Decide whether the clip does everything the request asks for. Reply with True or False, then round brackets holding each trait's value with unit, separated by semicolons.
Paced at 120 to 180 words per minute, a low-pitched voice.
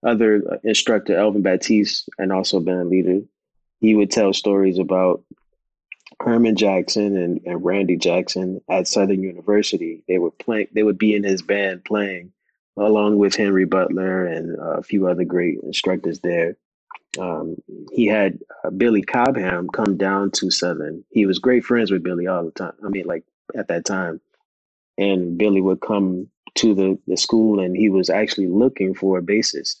True (170 wpm; 95 Hz)